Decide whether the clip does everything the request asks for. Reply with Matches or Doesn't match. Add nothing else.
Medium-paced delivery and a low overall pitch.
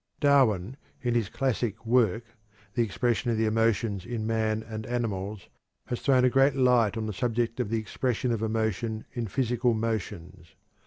Matches